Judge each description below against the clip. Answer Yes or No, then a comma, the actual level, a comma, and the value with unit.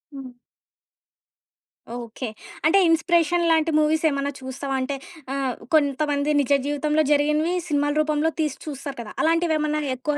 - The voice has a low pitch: No, very high, 300 Hz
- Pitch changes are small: Yes, narrow, 2.0 semitones